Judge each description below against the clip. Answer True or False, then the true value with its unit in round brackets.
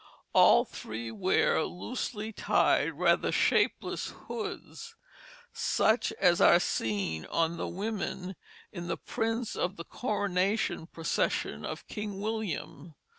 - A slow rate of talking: True (115 wpm)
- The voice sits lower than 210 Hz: True (185 Hz)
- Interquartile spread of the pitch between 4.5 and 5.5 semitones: True (4.9 semitones)